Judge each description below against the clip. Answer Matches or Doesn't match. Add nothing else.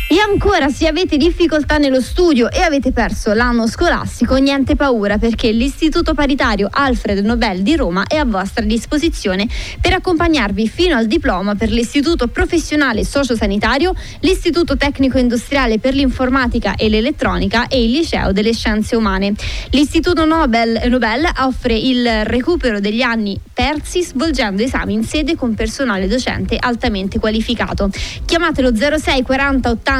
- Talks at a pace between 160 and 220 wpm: Doesn't match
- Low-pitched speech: Doesn't match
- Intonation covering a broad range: Doesn't match